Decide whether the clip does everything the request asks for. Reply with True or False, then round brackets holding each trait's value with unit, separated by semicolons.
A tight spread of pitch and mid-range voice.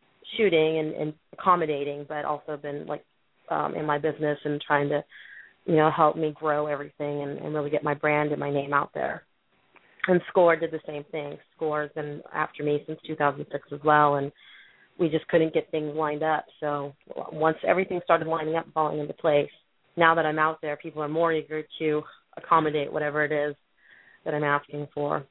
True (1.3 semitones; 150 Hz)